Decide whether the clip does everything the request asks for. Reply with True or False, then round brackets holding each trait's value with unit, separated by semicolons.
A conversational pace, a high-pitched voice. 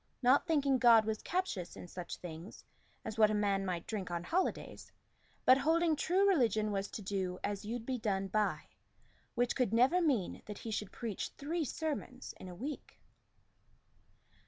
True (170 wpm; 225 Hz)